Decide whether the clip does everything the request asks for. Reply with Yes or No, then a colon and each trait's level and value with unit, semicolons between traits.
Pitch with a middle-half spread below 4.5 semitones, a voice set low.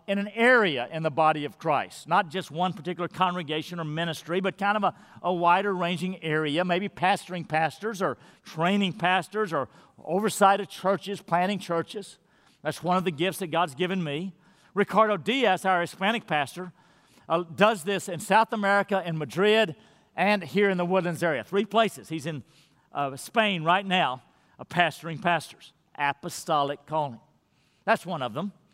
No: average, 3.4 semitones; medium, 180 Hz